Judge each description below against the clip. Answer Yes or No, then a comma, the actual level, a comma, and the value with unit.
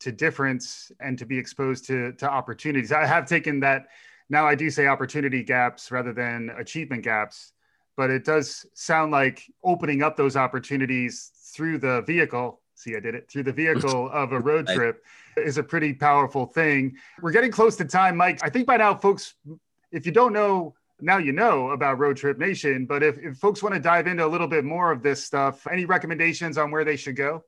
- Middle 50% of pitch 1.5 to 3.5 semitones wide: No, average, 3.9 semitones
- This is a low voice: No, medium, 150 Hz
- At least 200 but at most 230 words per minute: Yes, fast, 205 wpm